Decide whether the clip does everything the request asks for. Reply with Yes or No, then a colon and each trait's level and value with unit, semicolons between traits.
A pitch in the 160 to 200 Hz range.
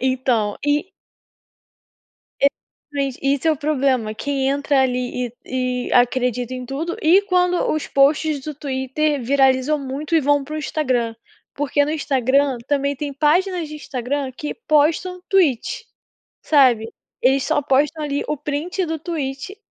No: very high, 280 Hz